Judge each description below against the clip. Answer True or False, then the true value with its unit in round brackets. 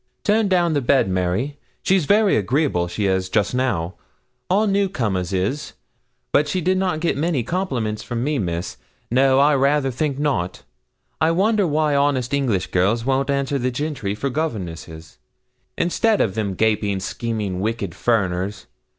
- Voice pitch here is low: True (130 Hz)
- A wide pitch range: True (7.3 semitones)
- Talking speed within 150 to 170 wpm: True (160 wpm)